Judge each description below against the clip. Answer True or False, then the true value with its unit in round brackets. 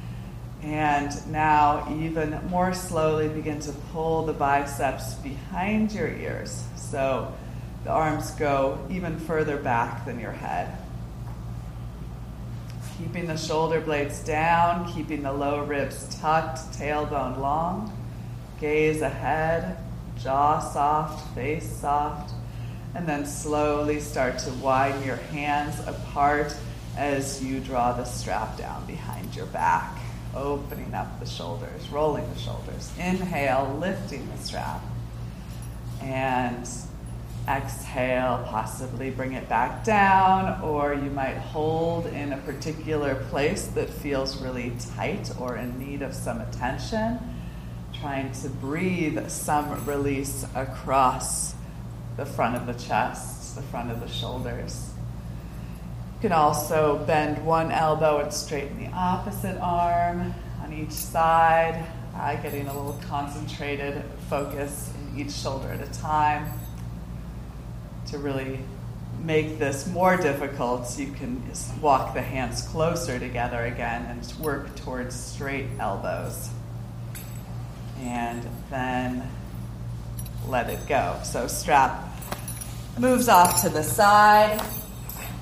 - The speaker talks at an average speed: False (120 wpm)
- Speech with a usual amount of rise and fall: True (4.3 semitones)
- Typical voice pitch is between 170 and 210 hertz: False (140 Hz)